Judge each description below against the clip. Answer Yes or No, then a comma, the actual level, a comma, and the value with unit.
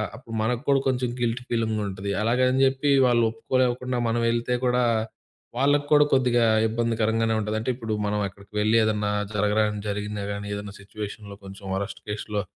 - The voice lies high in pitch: No, low, 115 Hz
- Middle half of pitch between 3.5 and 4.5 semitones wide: No, average, 2.9 semitones